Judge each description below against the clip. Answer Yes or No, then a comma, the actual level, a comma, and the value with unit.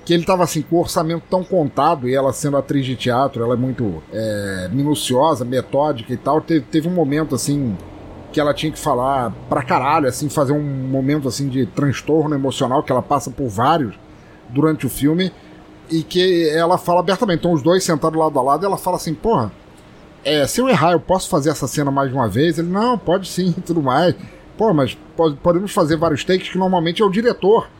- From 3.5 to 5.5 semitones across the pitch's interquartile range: Yes, average, 4.4 semitones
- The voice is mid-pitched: Yes, medium, 155 Hz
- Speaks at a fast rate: Yes, fast, 215 wpm